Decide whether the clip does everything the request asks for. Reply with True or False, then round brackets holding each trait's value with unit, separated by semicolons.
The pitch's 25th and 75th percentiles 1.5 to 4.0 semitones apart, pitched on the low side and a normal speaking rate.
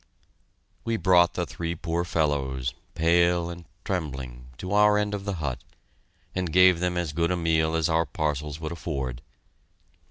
True (2.9 semitones; 85 Hz; 160 wpm)